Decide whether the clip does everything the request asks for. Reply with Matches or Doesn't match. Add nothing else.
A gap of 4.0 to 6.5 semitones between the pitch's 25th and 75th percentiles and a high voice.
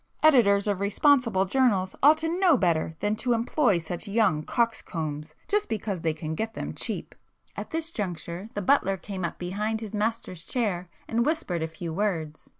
Matches